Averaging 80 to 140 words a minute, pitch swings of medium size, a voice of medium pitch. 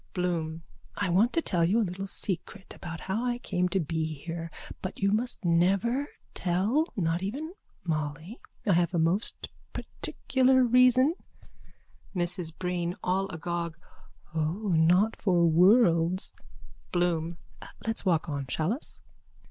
Yes: slow, 135 wpm; average, 4.1 semitones; medium, 180 Hz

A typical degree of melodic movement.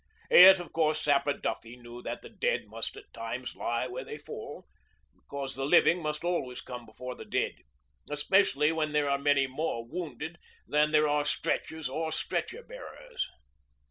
Yes: average, 3.6 semitones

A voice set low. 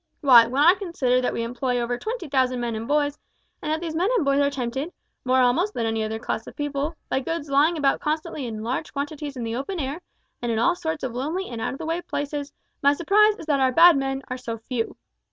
No: very high, 280 Hz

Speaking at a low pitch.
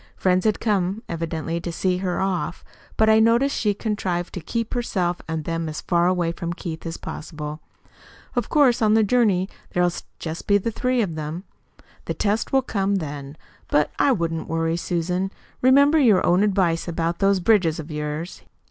No: medium, 180 Hz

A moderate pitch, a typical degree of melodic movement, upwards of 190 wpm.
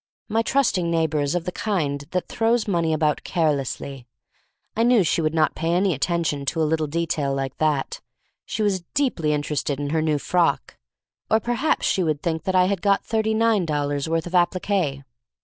Yes: medium, 165 Hz; average, 4.7 semitones; average, 200 wpm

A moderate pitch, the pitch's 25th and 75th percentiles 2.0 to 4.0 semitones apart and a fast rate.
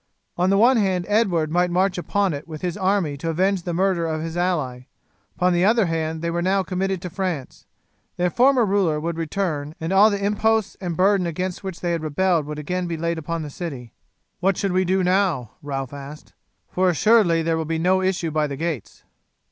Yes: medium, 175 Hz; average, 3.0 semitones; fast, 210 wpm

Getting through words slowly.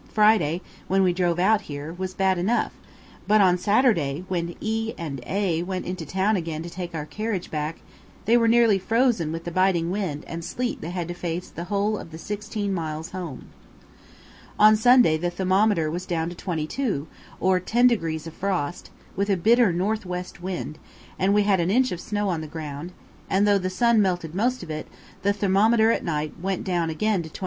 No: average, 200 wpm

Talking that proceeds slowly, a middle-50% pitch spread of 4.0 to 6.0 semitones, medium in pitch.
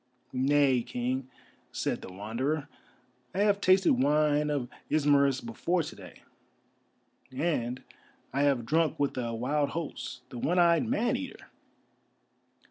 Yes: slow, 125 wpm; average, 4.6 semitones; medium, 145 Hz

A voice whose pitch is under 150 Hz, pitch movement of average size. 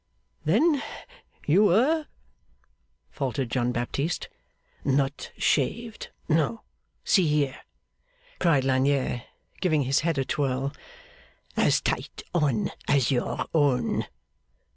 Yes: medium, 140 Hz; average, 4.2 semitones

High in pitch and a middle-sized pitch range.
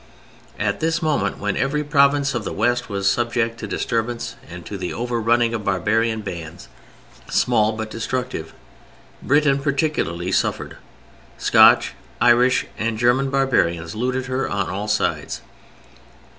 No: low, 115 Hz; average, 4.2 semitones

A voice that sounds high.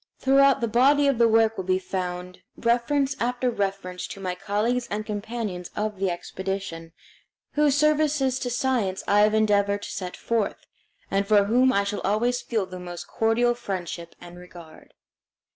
Yes: high, 210 Hz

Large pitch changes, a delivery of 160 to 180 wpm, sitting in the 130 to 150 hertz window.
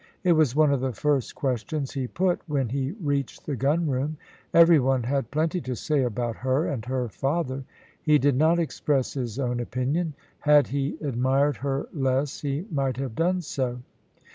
No: average, 2.8 semitones; average, 175 wpm; medium, 140 Hz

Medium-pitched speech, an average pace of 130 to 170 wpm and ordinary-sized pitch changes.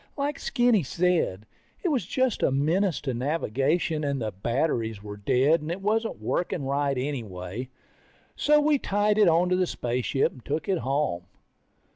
No: medium, 150 Hz; average, 160 wpm; wide, 7.4 semitones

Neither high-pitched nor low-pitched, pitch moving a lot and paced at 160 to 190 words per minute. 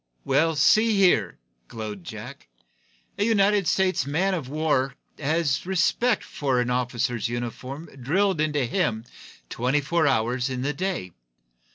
No: medium, 145 Hz; wide, 6.9 semitones; slow, 135 wpm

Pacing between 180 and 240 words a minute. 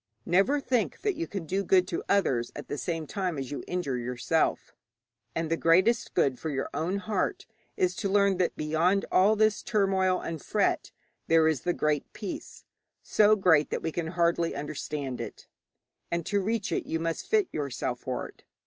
Yes: average, 185 wpm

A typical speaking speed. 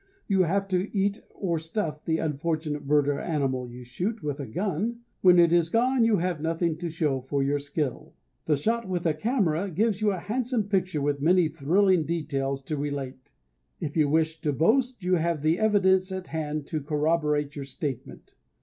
Yes: average, 190 wpm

